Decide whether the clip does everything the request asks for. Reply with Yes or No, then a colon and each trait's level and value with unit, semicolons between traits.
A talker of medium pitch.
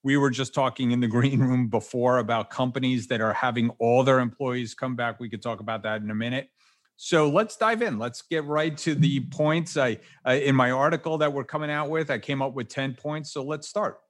No: low, 130 Hz